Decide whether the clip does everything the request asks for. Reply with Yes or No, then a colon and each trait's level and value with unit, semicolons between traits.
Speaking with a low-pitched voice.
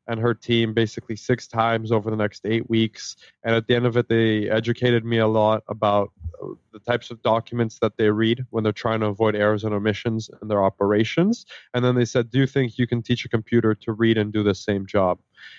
Yes: low, 115 Hz